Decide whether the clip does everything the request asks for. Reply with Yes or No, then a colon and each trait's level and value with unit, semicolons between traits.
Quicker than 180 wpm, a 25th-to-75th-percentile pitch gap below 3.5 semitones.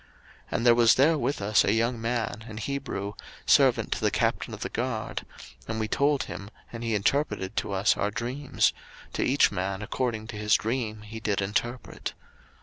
Yes: average, 190 wpm; average, 2.9 semitones